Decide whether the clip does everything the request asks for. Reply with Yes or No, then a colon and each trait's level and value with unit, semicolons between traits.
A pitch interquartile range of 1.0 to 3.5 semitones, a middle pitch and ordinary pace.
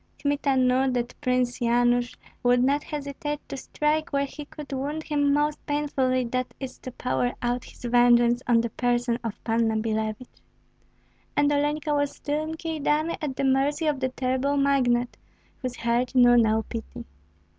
No: average, 3.0 semitones; very high, 260 Hz; average, 165 wpm